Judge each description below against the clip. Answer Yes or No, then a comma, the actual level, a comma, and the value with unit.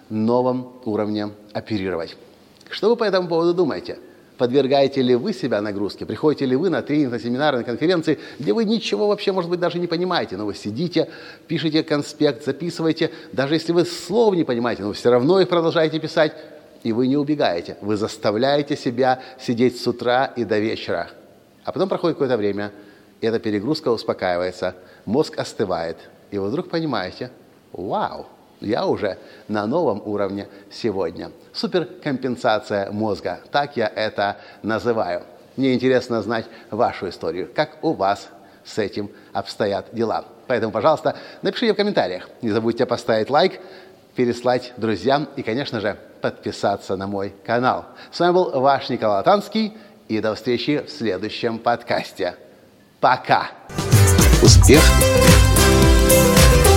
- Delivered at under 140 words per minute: No, average, 145 wpm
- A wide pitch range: Yes, wide, 7.1 semitones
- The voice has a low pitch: Yes, low, 125 Hz